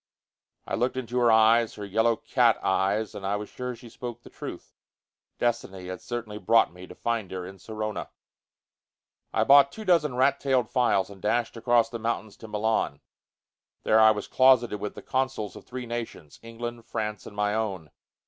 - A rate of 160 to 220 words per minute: Yes, average, 185 wpm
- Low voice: Yes, low, 115 Hz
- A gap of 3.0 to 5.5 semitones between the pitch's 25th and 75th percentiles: No, narrow, 2.6 semitones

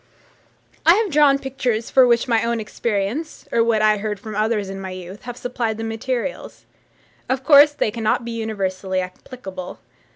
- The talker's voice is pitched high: Yes, high, 225 Hz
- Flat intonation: No, average, 3.6 semitones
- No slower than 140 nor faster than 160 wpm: No, average, 170 wpm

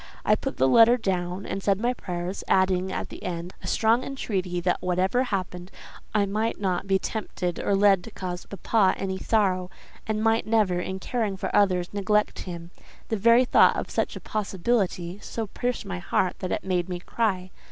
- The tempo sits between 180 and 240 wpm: Yes, average, 190 wpm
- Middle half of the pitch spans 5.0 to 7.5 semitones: No, average, 3.1 semitones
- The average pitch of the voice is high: Yes, high, 195 Hz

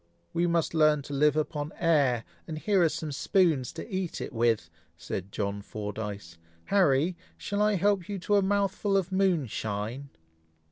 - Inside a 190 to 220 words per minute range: No, average, 160 wpm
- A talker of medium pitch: Yes, medium, 155 Hz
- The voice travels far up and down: Yes, wide, 8.0 semitones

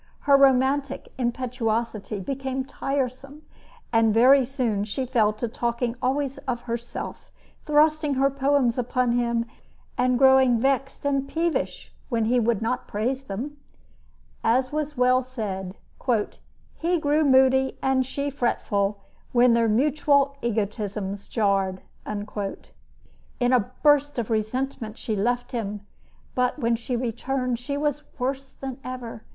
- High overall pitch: Yes, very high, 250 Hz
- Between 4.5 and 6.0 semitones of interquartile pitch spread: No, average, 3.0 semitones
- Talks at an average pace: No, slow, 130 wpm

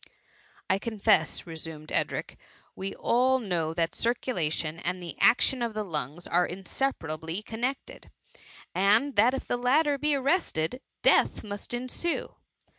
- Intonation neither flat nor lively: No, wide, 7.3 semitones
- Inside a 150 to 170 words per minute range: No, average, 140 wpm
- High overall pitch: Yes, high, 205 Hz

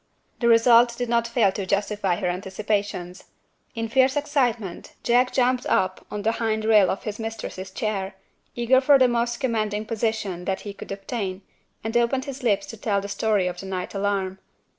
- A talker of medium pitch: No, high, 215 Hz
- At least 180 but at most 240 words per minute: Yes, average, 185 wpm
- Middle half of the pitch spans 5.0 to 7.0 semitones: No, average, 3.3 semitones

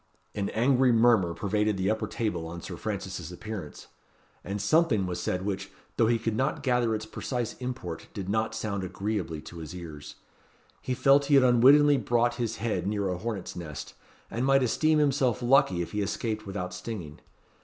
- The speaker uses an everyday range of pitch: Yes, average, 4.8 semitones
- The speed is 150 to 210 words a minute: Yes, average, 180 wpm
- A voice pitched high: No, low, 110 Hz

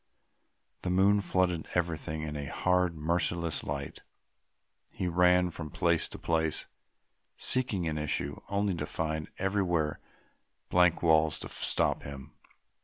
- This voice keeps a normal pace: No, slow, 125 wpm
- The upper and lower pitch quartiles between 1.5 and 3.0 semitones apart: Yes, average, 2.7 semitones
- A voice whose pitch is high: No, very low, 85 Hz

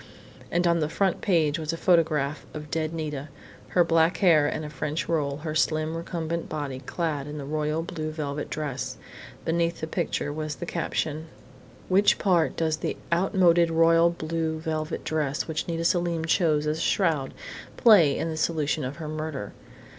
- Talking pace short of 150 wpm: No, average, 175 wpm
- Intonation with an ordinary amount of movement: No, narrow, 1.7 semitones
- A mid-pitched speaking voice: Yes, medium, 160 Hz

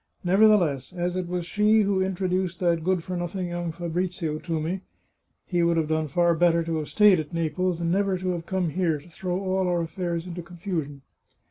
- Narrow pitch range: Yes, narrow, 1.9 semitones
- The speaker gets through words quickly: Yes, fast, 210 wpm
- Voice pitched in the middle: Yes, medium, 175 Hz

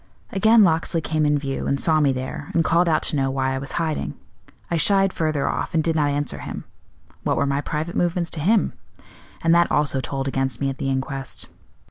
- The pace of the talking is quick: Yes, fast, 215 wpm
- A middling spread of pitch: Yes, average, 3.5 semitones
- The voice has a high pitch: No, medium, 150 Hz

